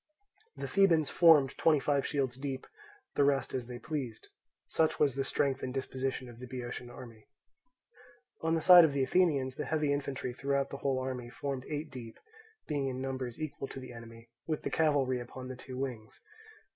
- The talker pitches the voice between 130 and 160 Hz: Yes, low, 135 Hz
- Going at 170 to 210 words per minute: Yes, average, 185 wpm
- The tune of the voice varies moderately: No, narrow, 2.3 semitones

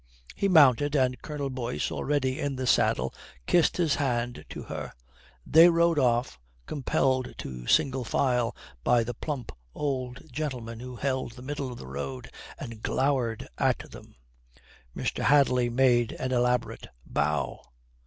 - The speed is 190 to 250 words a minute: No, average, 145 wpm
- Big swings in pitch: No, average, 3.0 semitones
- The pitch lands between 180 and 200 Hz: No, low, 130 Hz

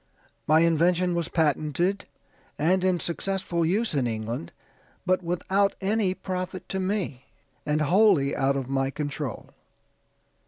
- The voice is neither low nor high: Yes, medium, 170 Hz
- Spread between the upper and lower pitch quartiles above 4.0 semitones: Yes, average, 4.5 semitones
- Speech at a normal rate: No, slow, 125 wpm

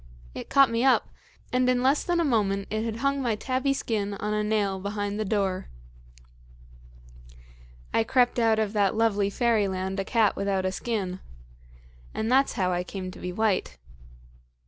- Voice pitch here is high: Yes, high, 215 Hz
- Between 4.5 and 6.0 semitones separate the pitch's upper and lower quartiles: No, average, 3.4 semitones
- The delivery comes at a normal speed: Yes, average, 170 wpm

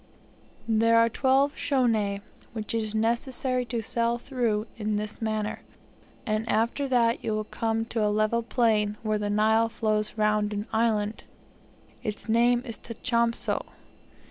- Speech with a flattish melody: Yes, narrow, 1.7 semitones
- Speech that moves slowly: No, average, 145 wpm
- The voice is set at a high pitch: Yes, high, 225 Hz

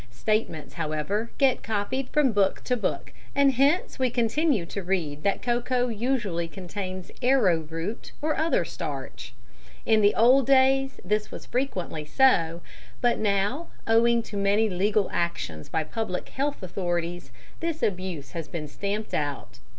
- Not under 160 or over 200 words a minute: No, average, 145 wpm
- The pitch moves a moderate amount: No, wide, 6.6 semitones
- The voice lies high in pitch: Yes, high, 205 Hz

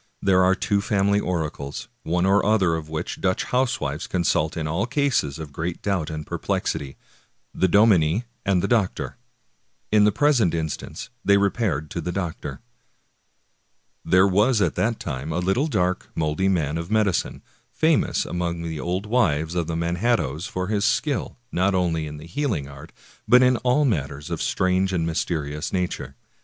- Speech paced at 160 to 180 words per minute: Yes, average, 170 wpm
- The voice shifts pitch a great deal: No, average, 4.6 semitones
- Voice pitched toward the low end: Yes, very low, 90 Hz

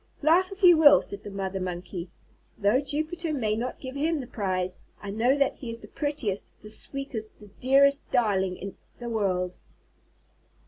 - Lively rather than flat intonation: Yes, wide, 6.3 semitones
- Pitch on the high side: Yes, high, 230 Hz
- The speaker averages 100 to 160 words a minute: No, average, 175 wpm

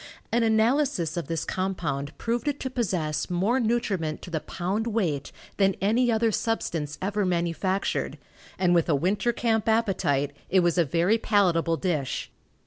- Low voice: No, high, 190 Hz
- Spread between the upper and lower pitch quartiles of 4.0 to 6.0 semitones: Yes, average, 5.2 semitones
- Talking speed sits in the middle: Yes, average, 155 wpm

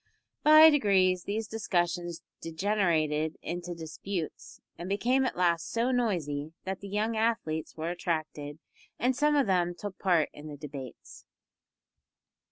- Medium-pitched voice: Yes, medium, 180 Hz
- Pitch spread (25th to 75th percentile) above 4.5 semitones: Yes, average, 5.3 semitones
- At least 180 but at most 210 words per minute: No, slow, 135 wpm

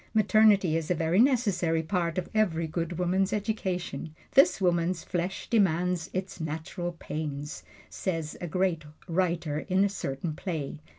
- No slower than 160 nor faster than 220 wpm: No, average, 140 wpm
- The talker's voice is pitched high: No, medium, 175 Hz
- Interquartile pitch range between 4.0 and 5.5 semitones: No, average, 3.0 semitones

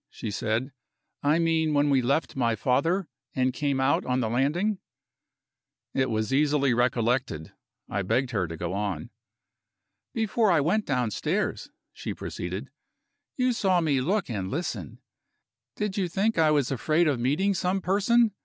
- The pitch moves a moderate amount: No, wide, 6.7 semitones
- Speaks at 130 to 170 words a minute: Yes, average, 155 wpm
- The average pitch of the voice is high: No, medium, 145 Hz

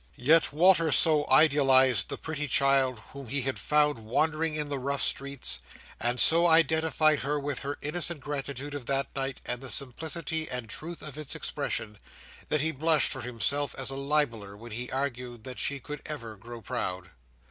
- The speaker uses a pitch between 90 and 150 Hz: Yes, medium, 140 Hz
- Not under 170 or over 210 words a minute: Yes, average, 180 wpm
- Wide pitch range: No, average, 3.4 semitones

